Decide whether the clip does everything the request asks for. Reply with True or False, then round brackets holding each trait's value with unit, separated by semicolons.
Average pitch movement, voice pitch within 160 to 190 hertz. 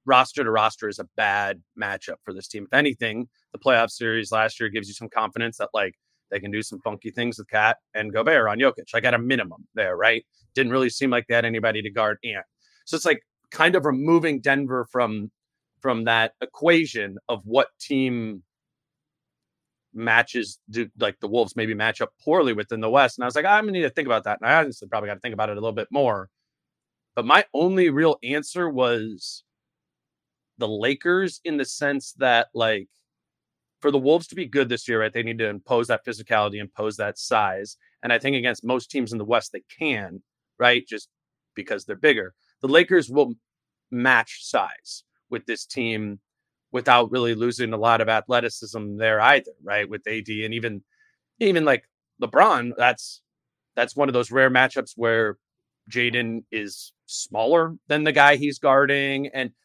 False (3.8 semitones; 120 Hz)